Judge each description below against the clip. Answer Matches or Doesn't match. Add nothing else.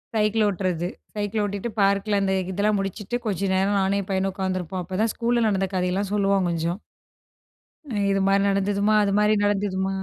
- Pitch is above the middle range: Matches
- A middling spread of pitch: Doesn't match